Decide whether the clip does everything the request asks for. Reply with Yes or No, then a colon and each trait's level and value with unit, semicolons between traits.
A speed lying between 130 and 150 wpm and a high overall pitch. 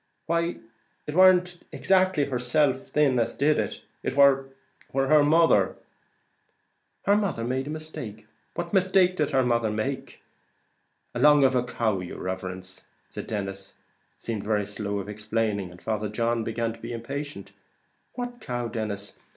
No: average, 145 wpm; low, 125 Hz